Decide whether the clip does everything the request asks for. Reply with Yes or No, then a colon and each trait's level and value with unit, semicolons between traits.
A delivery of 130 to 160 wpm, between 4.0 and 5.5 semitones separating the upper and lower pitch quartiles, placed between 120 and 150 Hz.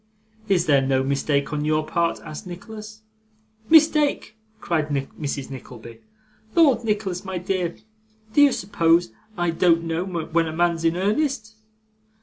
No: slow, 135 wpm; average, 5.2 semitones; medium, 170 Hz